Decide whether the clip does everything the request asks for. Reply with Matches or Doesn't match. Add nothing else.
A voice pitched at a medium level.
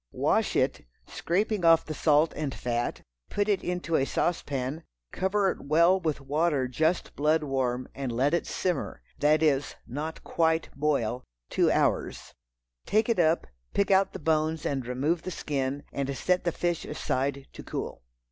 Matches